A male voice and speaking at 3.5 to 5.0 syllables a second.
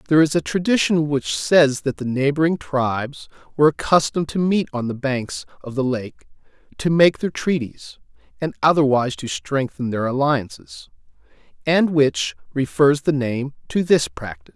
Yes: male; 4.9 syllables/s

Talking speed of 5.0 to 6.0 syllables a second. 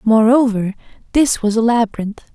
Yes: 5.2 syllables/s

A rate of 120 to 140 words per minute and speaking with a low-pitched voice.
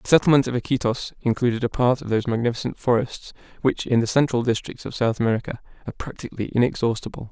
No: average, 180 wpm; low, 120 Hz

